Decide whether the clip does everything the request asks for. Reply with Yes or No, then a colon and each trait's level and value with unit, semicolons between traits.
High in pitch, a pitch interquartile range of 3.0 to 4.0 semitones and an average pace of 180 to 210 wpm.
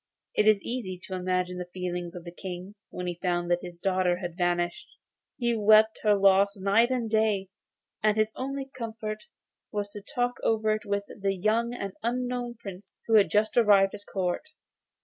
Yes: high, 205 Hz; average, 3.4 semitones; average, 190 wpm